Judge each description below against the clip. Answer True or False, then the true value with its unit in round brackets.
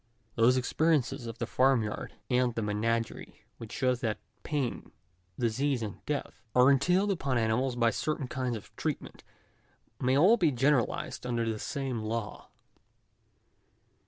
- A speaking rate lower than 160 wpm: True (140 wpm)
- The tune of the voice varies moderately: True (3.1 semitones)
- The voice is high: False (125 Hz)